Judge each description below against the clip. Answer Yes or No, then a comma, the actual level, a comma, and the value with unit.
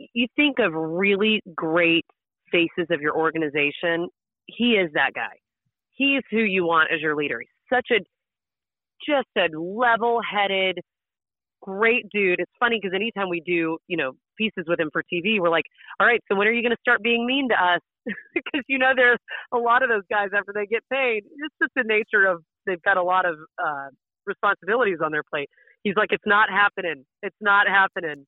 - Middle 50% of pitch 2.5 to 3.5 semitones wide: No, wide, 5.5 semitones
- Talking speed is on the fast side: No, average, 195 wpm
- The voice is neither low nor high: No, high, 200 Hz